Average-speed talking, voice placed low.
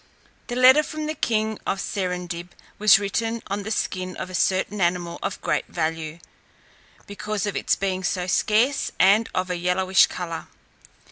No: average, 160 wpm; high, 190 Hz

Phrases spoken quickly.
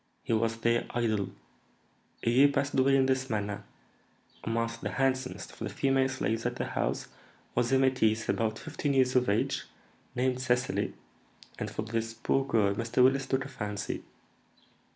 No: average, 165 wpm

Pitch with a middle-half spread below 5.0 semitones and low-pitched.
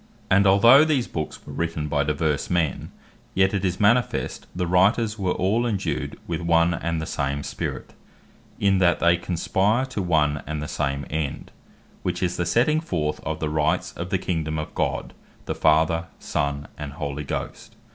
Yes: average, 4.0 semitones; very low, 85 Hz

